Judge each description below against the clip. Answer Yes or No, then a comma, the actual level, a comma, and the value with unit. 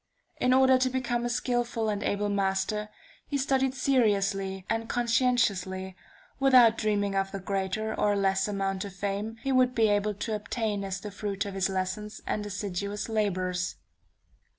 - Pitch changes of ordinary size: Yes, average, 3.4 semitones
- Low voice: No, high, 210 Hz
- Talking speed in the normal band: Yes, average, 160 wpm